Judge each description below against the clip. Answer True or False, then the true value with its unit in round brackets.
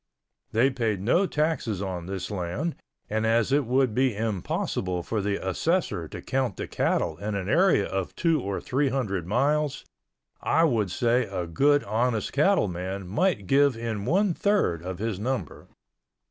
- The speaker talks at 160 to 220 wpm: True (165 wpm)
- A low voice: True (115 Hz)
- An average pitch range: False (6.3 semitones)